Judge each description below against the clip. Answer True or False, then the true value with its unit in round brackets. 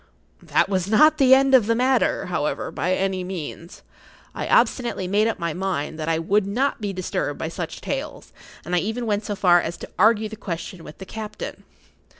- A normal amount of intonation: True (3.9 semitones)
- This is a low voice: False (195 Hz)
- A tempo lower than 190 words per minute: False (200 wpm)